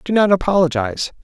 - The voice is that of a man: Yes, male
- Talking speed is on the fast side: No, average, 145 wpm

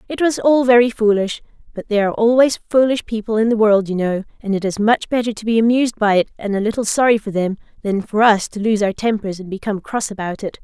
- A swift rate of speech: Yes, fast, 250 wpm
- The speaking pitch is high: Yes, high, 215 Hz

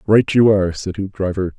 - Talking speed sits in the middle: Yes, average, 190 wpm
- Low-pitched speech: Yes, very low, 95 Hz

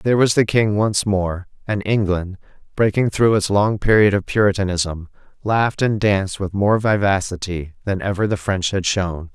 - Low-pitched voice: Yes, low, 100 Hz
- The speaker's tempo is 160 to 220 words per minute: Yes, average, 175 wpm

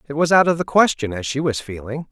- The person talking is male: Yes, male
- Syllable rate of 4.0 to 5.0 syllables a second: No, 6.2 syllables/s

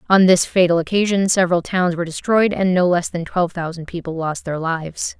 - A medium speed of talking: No, fast, 210 wpm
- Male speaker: No, female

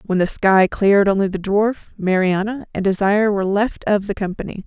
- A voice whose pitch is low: No, high, 200 Hz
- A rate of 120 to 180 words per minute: No, average, 195 wpm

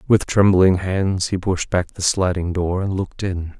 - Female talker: No, male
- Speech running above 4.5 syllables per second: No, 4.4 syllables/s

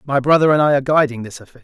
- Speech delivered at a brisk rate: Yes, fast, 295 wpm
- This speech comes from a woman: No, male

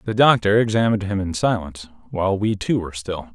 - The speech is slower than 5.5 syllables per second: No, 6.4 syllables/s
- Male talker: Yes, male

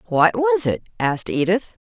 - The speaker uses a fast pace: No, average, 160 wpm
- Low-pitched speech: No, high, 190 Hz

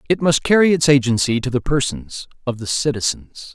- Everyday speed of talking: Yes, average, 185 wpm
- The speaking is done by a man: Yes, male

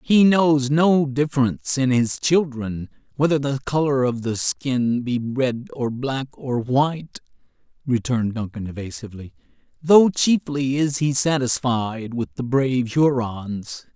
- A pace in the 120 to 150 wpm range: Yes, slow, 135 wpm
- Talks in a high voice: No, low, 130 Hz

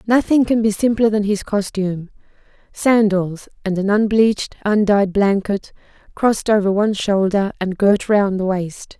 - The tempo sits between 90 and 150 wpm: Yes, average, 140 wpm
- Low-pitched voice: No, high, 205 Hz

